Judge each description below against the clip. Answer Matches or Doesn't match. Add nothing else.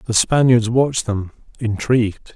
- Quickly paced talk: Doesn't match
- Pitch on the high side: Doesn't match